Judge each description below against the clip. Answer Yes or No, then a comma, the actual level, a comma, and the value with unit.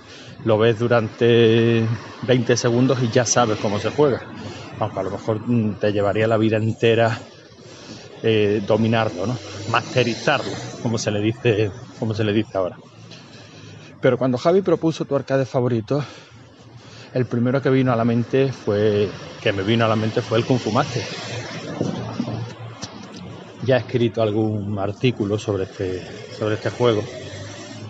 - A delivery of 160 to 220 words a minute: No, average, 145 wpm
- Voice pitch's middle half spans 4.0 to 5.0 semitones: No, narrow, 2.5 semitones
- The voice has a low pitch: Yes, low, 115 Hz